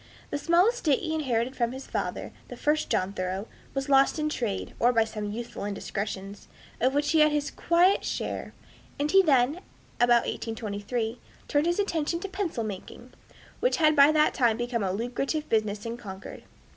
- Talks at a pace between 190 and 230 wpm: No, average, 180 wpm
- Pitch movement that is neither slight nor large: No, wide, 5.7 semitones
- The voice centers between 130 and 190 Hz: No, very high, 250 Hz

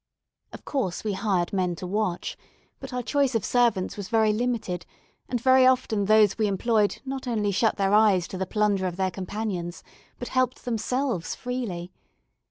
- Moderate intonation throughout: Yes, average, 4.5 semitones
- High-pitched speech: Yes, high, 210 Hz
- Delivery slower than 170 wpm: No, average, 175 wpm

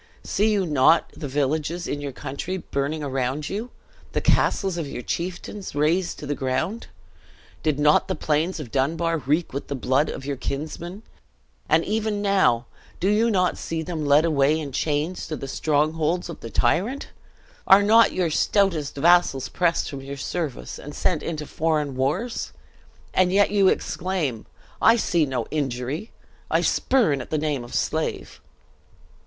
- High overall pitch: No, medium, 155 Hz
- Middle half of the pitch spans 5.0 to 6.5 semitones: No, average, 4.6 semitones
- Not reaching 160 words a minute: No, average, 165 wpm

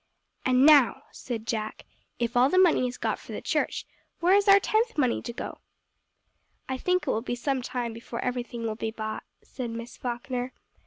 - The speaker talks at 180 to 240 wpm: Yes, average, 200 wpm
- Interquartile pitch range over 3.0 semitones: Yes, average, 3.4 semitones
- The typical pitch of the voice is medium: No, very high, 250 Hz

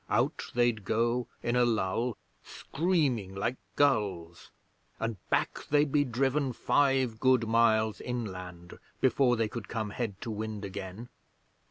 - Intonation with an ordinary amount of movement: Yes, average, 3.5 semitones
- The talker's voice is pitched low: Yes, low, 115 Hz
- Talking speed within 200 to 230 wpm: No, slow, 135 wpm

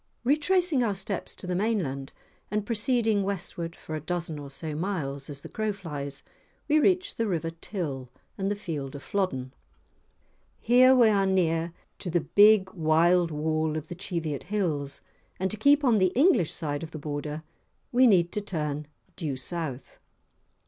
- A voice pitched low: No, medium, 175 Hz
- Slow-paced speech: No, average, 170 wpm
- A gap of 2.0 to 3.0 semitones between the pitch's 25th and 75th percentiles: No, wide, 5.5 semitones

